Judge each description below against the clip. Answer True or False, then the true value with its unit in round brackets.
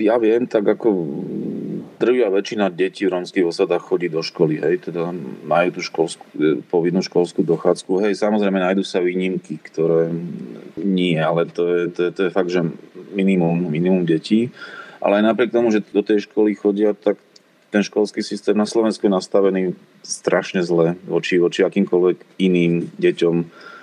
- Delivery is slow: False (160 wpm)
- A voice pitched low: True (95 Hz)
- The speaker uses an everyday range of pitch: True (3.1 semitones)